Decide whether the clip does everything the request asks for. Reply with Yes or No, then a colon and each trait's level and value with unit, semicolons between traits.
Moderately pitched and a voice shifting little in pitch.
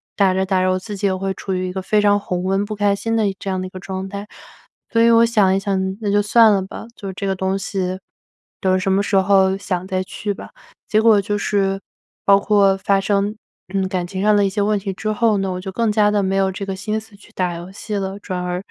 No: high, 195 Hz; narrow, 1.5 semitones